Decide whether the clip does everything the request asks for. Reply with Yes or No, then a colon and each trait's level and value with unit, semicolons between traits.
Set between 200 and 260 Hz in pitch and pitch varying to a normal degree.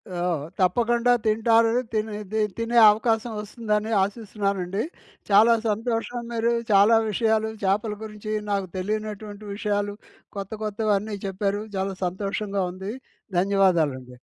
No: high, 210 Hz; narrow, 2.0 semitones